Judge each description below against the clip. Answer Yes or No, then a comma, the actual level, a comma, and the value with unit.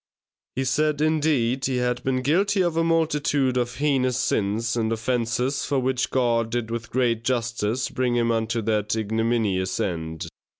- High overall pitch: No, low, 120 Hz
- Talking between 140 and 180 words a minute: Yes, average, 160 wpm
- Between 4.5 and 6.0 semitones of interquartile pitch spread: No, average, 2.9 semitones